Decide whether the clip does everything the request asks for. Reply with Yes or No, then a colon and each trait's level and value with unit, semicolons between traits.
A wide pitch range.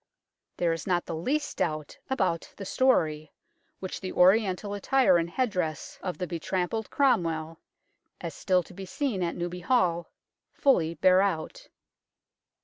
No: average, 3.6 semitones